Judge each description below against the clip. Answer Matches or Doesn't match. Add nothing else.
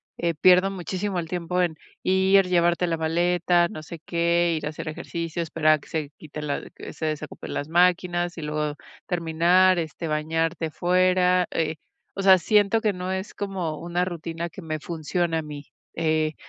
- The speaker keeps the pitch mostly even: Matches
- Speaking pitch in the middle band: Matches